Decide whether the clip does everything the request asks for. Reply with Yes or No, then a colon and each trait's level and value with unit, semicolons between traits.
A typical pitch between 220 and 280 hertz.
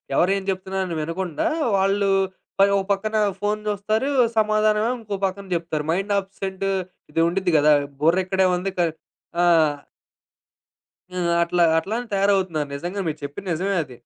No: high, 190 Hz